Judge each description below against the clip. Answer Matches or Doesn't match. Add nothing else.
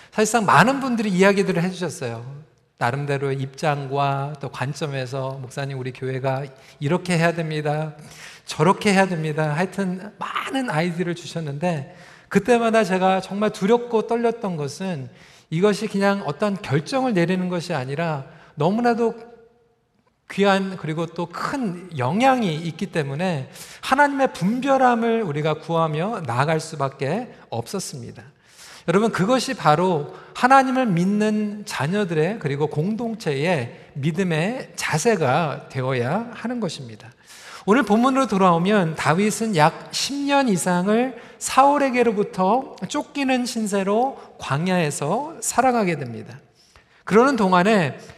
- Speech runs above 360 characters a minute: Doesn't match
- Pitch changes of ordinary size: Doesn't match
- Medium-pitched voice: Matches